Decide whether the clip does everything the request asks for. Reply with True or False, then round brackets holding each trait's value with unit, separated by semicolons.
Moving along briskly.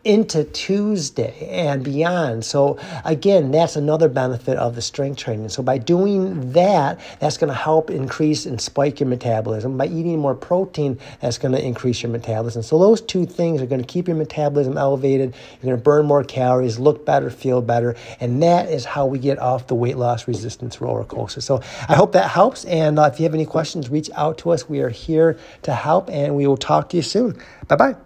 True (210 wpm)